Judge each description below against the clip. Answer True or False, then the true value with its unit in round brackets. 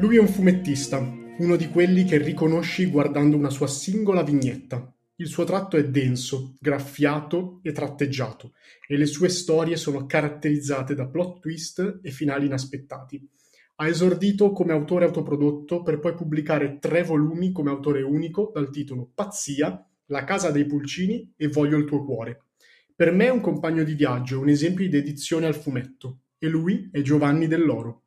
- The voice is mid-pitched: True (150 Hz)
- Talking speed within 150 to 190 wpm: True (165 wpm)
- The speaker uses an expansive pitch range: False (3.4 semitones)